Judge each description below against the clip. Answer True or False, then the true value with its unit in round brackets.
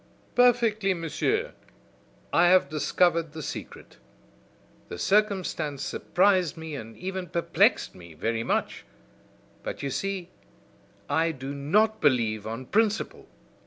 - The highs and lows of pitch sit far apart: True (6.0 semitones)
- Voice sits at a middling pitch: True (165 Hz)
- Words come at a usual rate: False (115 wpm)